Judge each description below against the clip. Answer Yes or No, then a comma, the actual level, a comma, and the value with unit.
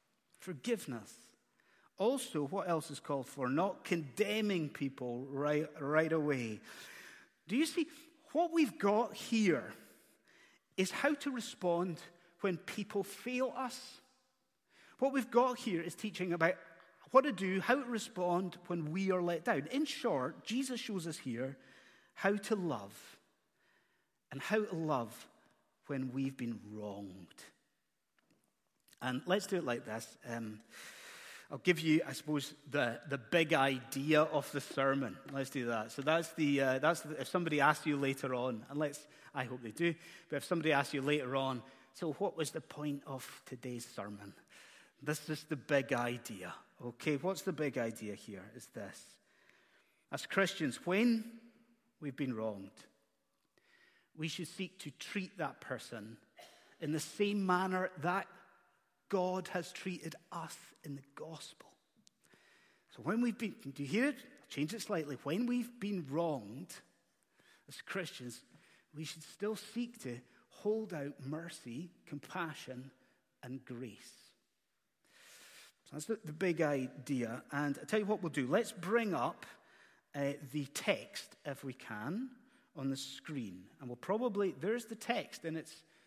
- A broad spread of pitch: Yes, wide, 6.4 semitones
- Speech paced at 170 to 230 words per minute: No, average, 150 wpm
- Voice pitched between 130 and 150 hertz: No, medium, 160 Hz